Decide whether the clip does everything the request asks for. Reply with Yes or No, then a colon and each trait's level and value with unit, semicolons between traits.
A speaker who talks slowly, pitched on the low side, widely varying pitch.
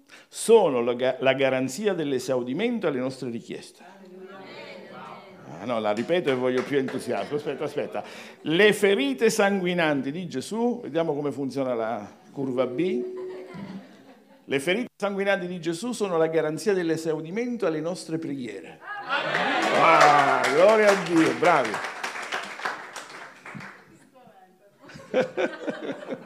No: slow, 105 wpm; medium, 165 Hz; wide, 6.9 semitones